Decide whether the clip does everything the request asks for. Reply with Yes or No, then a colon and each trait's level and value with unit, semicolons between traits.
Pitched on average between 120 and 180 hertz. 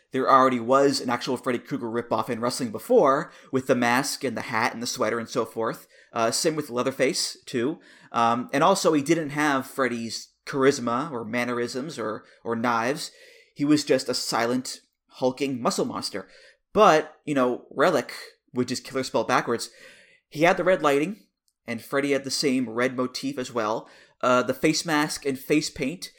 Yes: low, 135 Hz